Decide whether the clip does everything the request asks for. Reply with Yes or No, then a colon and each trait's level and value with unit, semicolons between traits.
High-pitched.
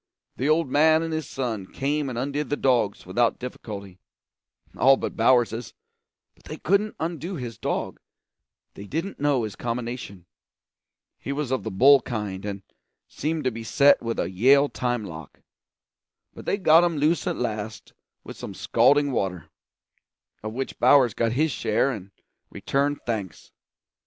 No: low, 125 Hz